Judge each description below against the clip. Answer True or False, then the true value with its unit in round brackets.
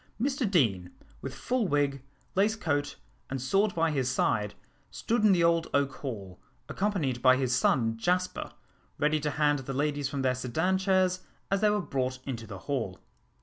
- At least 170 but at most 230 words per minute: True (175 wpm)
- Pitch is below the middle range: False (145 Hz)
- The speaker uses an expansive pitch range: True (6.3 semitones)